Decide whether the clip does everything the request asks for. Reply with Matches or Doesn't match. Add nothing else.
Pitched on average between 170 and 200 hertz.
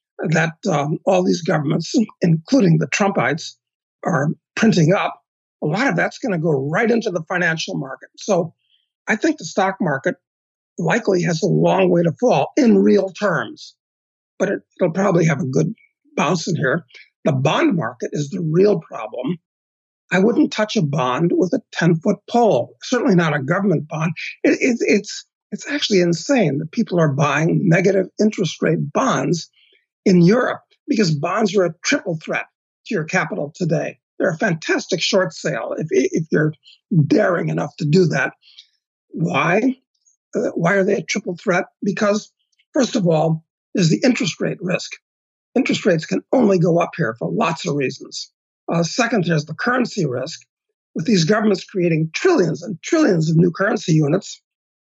Matches